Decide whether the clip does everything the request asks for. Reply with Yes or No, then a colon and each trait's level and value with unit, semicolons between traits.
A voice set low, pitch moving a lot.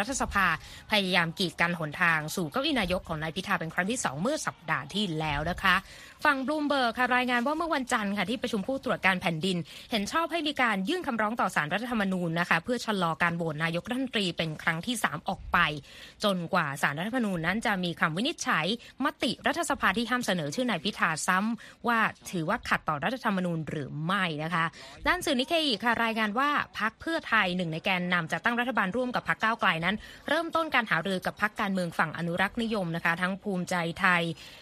No: high, 200 Hz; wide, 6.3 semitones